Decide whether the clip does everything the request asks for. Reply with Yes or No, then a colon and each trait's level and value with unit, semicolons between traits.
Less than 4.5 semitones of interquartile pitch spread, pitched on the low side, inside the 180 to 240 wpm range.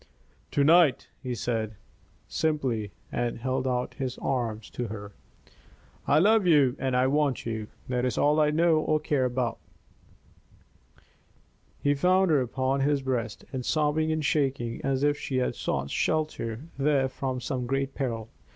No: average, 3.4 semitones; low, 130 Hz; average, 150 wpm